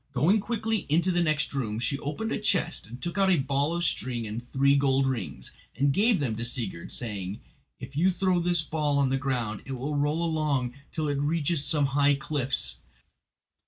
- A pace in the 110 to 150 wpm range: No, average, 195 wpm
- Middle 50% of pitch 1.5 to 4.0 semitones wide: No, average, 4.6 semitones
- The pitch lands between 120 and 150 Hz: Yes, medium, 140 Hz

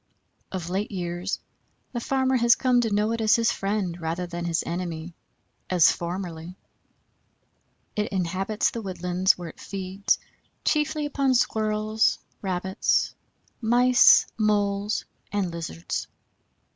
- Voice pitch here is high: Yes, high, 195 Hz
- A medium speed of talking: No, slow, 120 wpm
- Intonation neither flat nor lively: Yes, average, 3.9 semitones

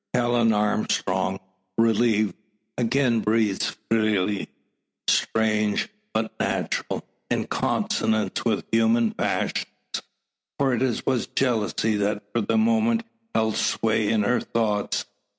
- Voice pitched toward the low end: Yes, low, 110 Hz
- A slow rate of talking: Yes, slow, 105 wpm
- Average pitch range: No, narrow, 2.1 semitones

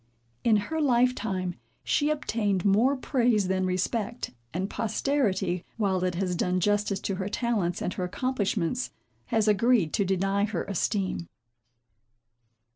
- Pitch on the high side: Yes, high, 205 Hz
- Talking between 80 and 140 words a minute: Yes, slow, 135 wpm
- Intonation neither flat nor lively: Yes, average, 4.1 semitones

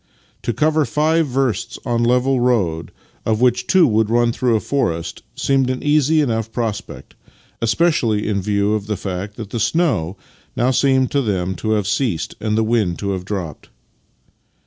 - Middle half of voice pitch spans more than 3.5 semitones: Yes, average, 4.3 semitones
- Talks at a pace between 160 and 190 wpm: Yes, average, 170 wpm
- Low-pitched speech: Yes, low, 115 Hz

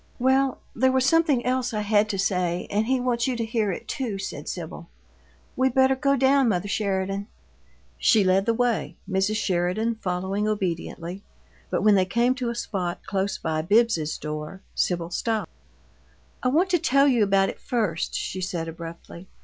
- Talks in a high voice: Yes, high, 210 Hz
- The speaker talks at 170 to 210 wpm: Yes, average, 175 wpm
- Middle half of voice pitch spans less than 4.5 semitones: No, average, 5.1 semitones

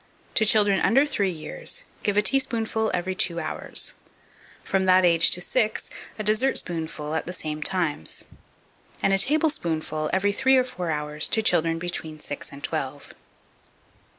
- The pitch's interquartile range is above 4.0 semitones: Yes, wide, 5.4 semitones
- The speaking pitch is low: No, medium, 185 Hz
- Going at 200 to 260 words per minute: No, average, 150 wpm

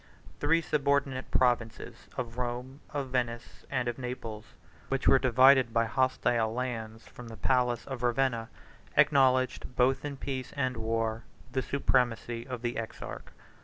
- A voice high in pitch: No, low, 125 Hz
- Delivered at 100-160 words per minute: Yes, average, 140 wpm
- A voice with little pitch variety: Yes, narrow, 2.3 semitones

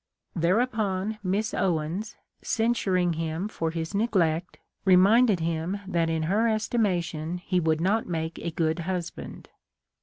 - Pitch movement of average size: Yes, average, 4.2 semitones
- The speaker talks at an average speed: No, slow, 125 wpm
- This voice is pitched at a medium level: Yes, medium, 180 Hz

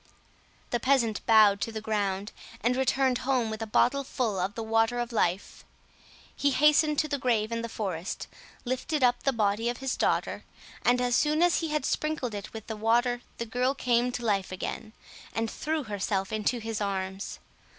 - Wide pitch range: No, average, 3.3 semitones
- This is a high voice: Yes, high, 230 Hz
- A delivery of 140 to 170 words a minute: No, average, 190 wpm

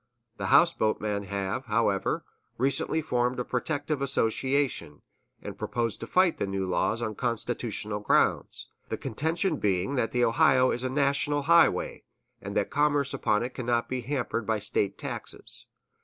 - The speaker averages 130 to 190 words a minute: Yes, average, 155 wpm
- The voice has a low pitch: Yes, low, 125 Hz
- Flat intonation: No, average, 4.7 semitones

